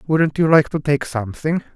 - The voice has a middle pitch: Yes, medium, 150 Hz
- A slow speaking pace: No, fast, 205 wpm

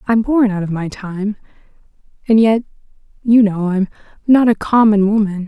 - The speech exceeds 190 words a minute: No, average, 165 wpm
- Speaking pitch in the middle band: No, high, 210 Hz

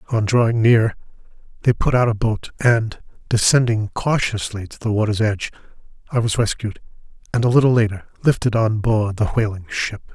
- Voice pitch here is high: No, low, 110 Hz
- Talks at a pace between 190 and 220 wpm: No, average, 165 wpm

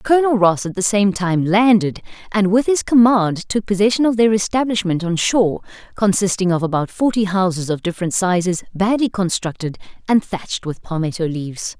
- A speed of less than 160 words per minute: No, average, 170 wpm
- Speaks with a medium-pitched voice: No, high, 195 Hz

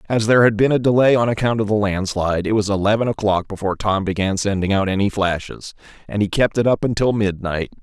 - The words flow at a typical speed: No, fast, 220 wpm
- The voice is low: Yes, low, 105 Hz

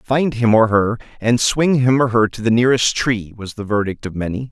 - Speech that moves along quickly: Yes, fast, 240 wpm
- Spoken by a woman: No, male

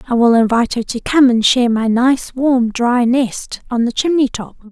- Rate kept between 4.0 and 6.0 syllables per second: Yes, 4.9 syllables/s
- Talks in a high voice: Yes, high, 245 Hz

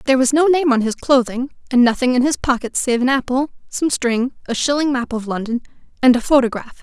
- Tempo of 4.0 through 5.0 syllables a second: No, 5.8 syllables/s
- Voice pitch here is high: Yes, very high, 255 Hz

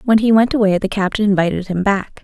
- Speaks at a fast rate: Yes, fast, 240 wpm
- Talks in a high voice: Yes, high, 205 Hz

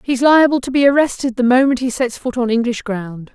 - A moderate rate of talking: No, fast, 235 wpm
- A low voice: No, very high, 250 Hz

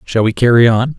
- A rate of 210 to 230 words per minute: No, fast, 245 wpm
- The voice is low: Yes, low, 115 Hz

